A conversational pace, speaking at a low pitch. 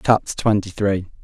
Yes: average, 145 wpm; low, 100 Hz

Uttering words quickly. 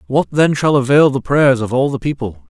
Yes: fast, 230 wpm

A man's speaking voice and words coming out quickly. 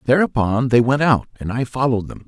Yes: male; fast, 210 wpm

